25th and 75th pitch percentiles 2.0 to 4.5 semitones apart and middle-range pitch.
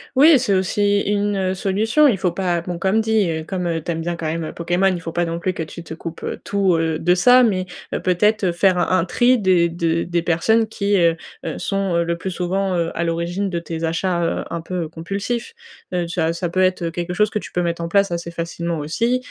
Yes: average, 2.8 semitones; medium, 180 Hz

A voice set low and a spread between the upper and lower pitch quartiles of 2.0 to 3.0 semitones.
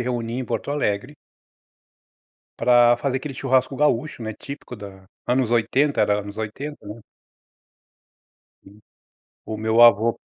No: low, 120 Hz; average, 3.5 semitones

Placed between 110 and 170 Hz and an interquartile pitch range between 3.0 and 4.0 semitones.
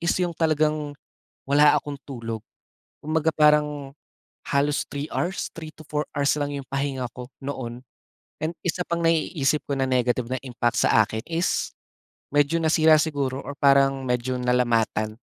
Yes: medium, 140 Hz; average, 3.3 semitones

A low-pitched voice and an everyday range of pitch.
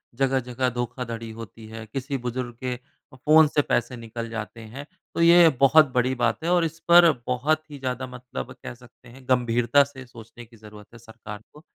Yes: low, 125 Hz; average, 3.0 semitones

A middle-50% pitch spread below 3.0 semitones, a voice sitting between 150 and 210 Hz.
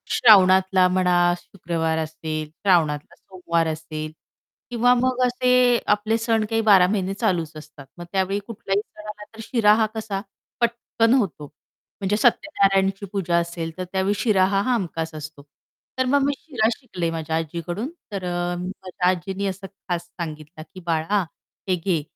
No: average, 4.3 semitones; high, 190 Hz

